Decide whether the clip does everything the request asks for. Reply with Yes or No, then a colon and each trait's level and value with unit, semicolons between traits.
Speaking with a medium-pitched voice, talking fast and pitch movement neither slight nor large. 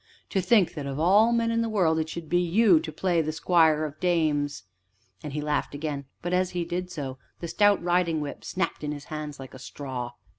Yes: medium, 160 Hz; fast, 225 wpm; average, 3.5 semitones